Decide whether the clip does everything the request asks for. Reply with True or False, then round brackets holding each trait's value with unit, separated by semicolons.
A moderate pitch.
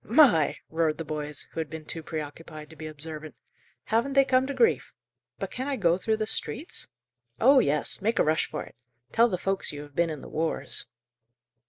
True (165 Hz)